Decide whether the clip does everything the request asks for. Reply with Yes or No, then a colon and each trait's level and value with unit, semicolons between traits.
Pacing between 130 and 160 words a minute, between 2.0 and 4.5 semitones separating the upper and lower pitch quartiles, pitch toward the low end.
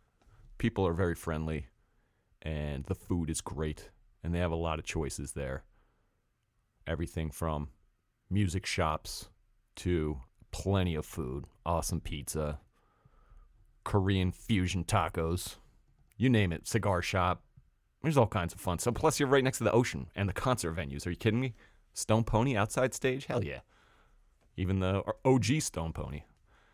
No: average, 150 wpm; average, 5.1 semitones; very low, 90 Hz